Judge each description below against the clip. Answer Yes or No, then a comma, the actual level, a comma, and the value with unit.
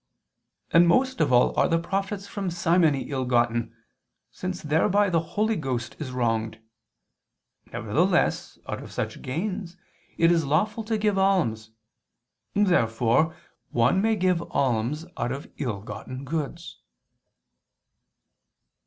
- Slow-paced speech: Yes, slow, 125 wpm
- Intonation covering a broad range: Yes, wide, 7.4 semitones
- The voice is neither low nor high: Yes, medium, 165 Hz